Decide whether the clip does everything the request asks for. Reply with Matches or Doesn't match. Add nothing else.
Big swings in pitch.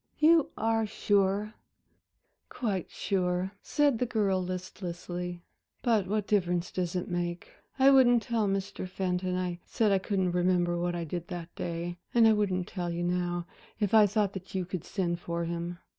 Doesn't match